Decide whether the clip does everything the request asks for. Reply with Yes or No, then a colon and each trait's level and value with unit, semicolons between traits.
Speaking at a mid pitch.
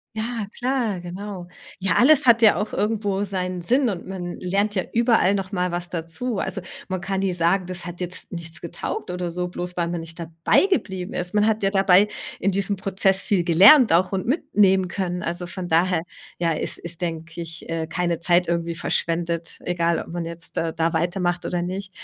Yes: medium, 180 Hz